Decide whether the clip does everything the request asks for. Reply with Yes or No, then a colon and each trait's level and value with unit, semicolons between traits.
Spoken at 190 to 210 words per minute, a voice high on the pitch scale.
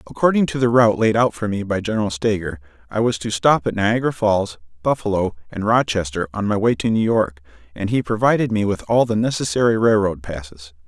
No: fast, 205 wpm; low, 105 Hz